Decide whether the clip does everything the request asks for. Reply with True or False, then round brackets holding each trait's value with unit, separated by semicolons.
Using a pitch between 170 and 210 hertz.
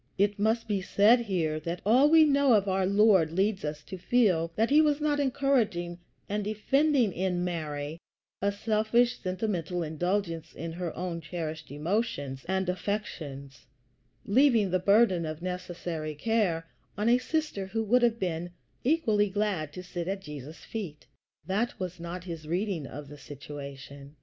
True (185 Hz)